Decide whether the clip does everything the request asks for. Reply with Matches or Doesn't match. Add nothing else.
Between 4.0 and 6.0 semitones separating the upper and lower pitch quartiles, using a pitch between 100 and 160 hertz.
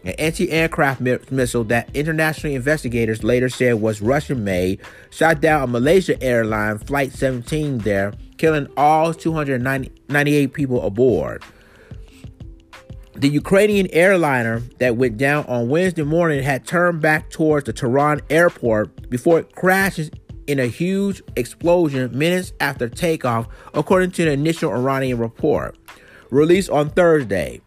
Matches